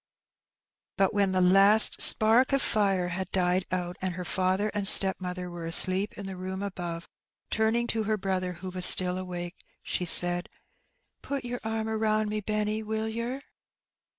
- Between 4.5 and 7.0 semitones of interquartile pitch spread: No, average, 3.0 semitones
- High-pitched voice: Yes, high, 195 Hz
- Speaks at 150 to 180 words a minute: Yes, average, 165 wpm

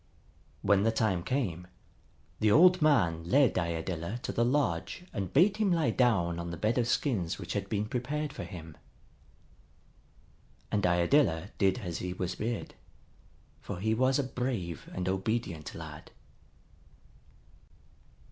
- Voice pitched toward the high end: No, low, 105 Hz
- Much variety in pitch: Yes, wide, 6.7 semitones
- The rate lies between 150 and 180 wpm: No, average, 140 wpm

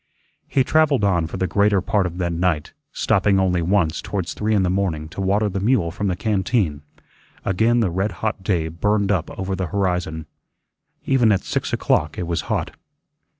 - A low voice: Yes, very low, 95 Hz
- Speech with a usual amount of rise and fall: Yes, average, 3.0 semitones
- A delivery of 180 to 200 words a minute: Yes, average, 190 wpm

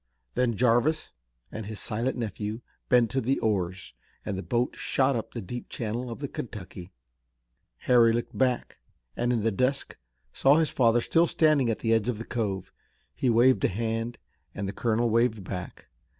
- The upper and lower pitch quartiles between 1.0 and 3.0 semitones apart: Yes, narrow, 2.6 semitones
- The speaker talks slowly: No, average, 180 wpm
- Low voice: Yes, low, 115 Hz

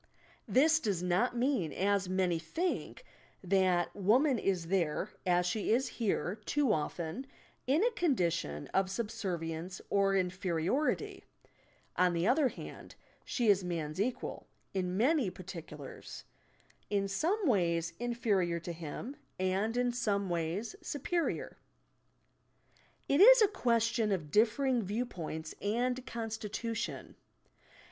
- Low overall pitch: No, high, 200 Hz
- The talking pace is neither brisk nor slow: No, slow, 125 wpm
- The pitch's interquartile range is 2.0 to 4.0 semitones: No, wide, 5.5 semitones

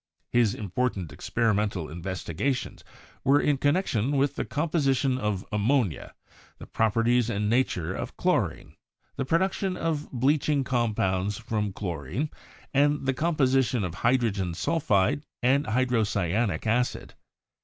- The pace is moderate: No, slow, 120 wpm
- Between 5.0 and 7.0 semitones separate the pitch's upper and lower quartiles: Yes, wide, 5.4 semitones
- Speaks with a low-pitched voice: Yes, low, 120 Hz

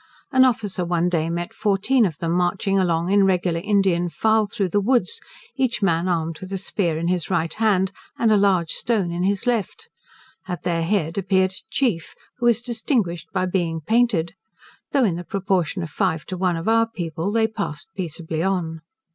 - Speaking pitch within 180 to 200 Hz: Yes, medium, 185 Hz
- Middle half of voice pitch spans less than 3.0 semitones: No, average, 3.8 semitones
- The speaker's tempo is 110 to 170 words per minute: No, average, 195 wpm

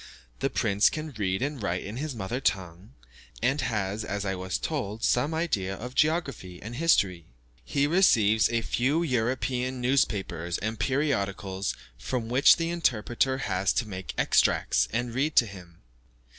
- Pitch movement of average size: No, wide, 5.8 semitones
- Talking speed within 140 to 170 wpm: Yes, average, 155 wpm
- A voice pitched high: No, low, 115 Hz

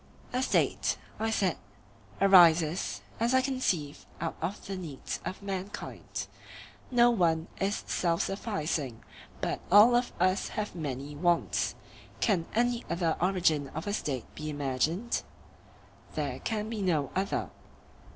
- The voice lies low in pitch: No, medium, 185 Hz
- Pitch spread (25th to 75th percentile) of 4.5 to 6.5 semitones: Yes, average, 4.9 semitones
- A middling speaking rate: No, slow, 130 wpm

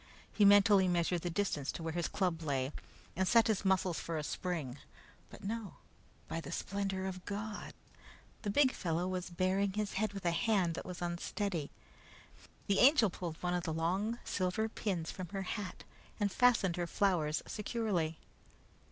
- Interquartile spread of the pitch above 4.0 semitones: No, average, 3.2 semitones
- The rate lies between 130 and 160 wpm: No, average, 170 wpm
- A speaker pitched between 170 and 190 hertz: Yes, medium, 185 Hz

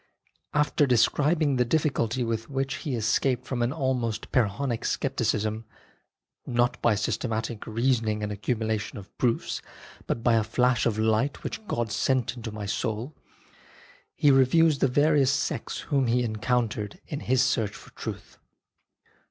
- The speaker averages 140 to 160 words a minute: Yes, average, 145 wpm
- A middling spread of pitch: Yes, average, 3.4 semitones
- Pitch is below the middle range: Yes, low, 120 Hz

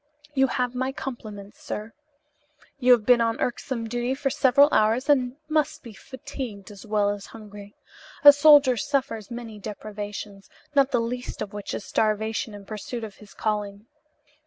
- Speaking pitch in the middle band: No, high, 230 Hz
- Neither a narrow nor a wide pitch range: Yes, average, 3.8 semitones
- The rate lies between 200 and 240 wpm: No, average, 160 wpm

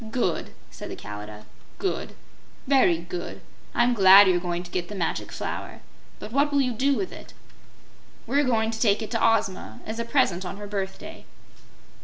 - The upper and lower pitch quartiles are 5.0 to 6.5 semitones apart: Yes, wide, 5.6 semitones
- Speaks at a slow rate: No, average, 180 wpm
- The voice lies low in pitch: No, high, 205 Hz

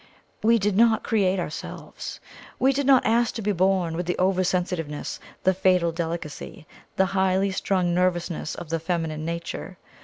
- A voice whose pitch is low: No, medium, 185 Hz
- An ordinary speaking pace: Yes, average, 160 wpm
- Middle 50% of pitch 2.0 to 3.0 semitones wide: Yes, narrow, 2.6 semitones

